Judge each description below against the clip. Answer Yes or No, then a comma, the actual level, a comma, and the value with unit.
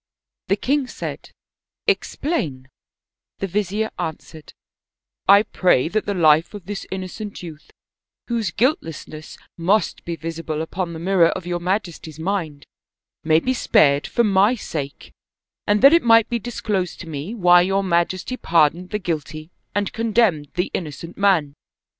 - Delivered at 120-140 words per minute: No, average, 155 wpm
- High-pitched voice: No, medium, 180 Hz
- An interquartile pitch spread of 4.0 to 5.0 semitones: Yes, average, 4.4 semitones